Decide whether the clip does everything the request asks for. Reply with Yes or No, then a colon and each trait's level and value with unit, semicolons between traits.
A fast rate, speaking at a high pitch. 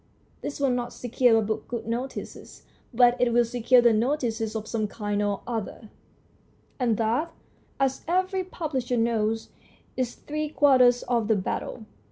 No: average, 155 wpm; high, 240 Hz